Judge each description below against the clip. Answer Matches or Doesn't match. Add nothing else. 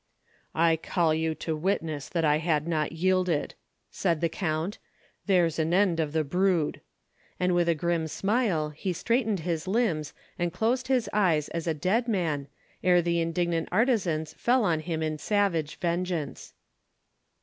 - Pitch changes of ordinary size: Matches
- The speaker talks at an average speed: Matches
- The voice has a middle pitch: Matches